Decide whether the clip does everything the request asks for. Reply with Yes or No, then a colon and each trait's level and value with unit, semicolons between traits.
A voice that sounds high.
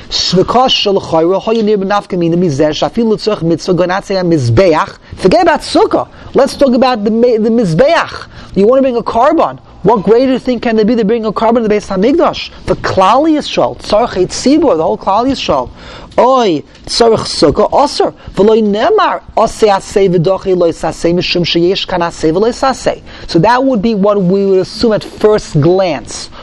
Yes: high, 210 Hz